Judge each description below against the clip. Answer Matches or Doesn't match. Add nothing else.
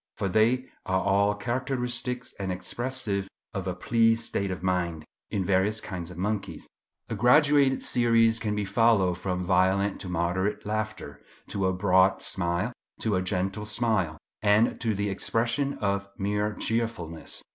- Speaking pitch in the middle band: Doesn't match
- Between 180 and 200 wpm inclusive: Doesn't match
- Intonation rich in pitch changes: Doesn't match